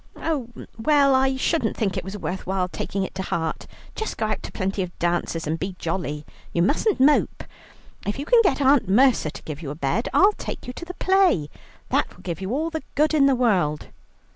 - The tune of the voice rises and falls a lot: Yes, wide, 8.5 semitones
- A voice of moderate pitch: No, high, 215 Hz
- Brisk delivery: Yes, fast, 220 wpm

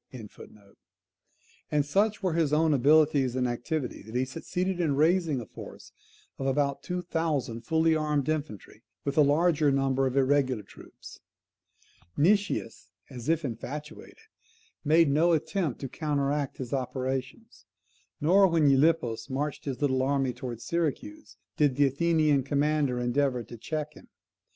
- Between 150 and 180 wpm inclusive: No, average, 140 wpm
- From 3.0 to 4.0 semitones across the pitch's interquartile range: Yes, average, 3.4 semitones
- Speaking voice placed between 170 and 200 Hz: No, medium, 145 Hz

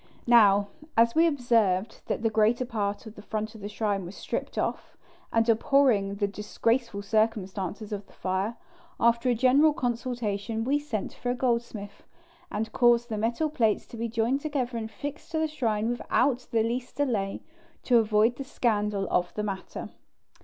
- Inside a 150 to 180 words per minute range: Yes, average, 175 wpm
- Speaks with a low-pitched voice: No, high, 225 Hz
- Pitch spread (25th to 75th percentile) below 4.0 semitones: Yes, average, 2.9 semitones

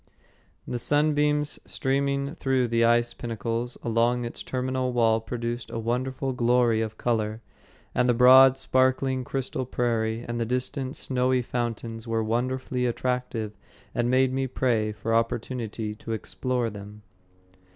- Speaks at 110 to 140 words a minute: Yes, slow, 135 wpm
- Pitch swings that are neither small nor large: No, narrow, 2.1 semitones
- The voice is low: Yes, low, 120 Hz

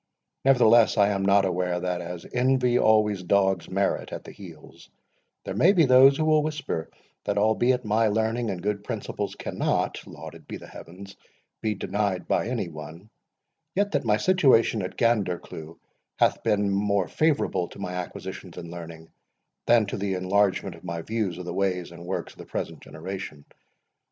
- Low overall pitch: Yes, low, 100 Hz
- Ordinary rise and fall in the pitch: Yes, average, 4.4 semitones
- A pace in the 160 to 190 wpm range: Yes, average, 170 wpm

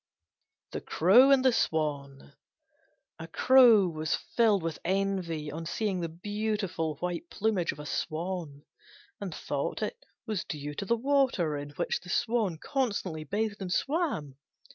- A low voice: No, medium, 185 Hz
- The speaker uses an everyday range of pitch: No, wide, 5.9 semitones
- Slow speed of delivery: No, average, 145 wpm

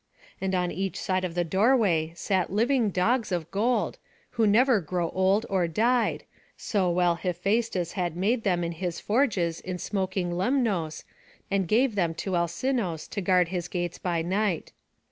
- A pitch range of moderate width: Yes, average, 3.6 semitones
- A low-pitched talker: No, medium, 185 Hz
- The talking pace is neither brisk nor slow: Yes, average, 165 wpm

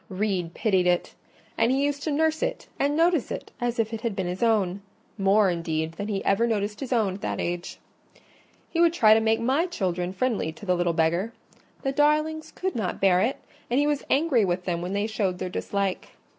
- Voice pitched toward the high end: Yes, high, 215 Hz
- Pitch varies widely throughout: Yes, wide, 6.8 semitones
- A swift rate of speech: Yes, fast, 215 wpm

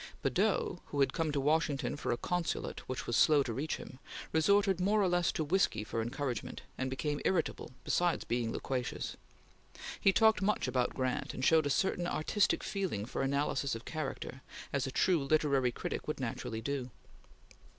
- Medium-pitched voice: Yes, medium, 145 Hz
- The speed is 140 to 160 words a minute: No, average, 175 wpm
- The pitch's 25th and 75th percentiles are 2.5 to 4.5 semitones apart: No, average, 5.2 semitones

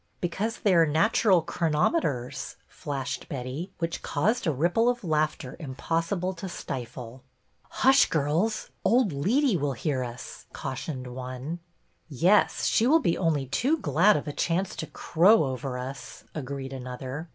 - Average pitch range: No, wide, 6.0 semitones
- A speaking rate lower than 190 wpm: Yes, average, 150 wpm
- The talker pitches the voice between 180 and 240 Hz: No, medium, 155 Hz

